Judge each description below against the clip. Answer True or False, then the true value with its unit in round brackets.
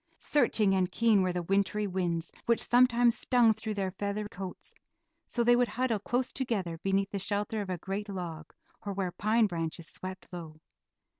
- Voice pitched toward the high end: True (200 Hz)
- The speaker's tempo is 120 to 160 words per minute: False (175 wpm)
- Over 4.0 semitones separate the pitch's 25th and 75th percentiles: False (3.6 semitones)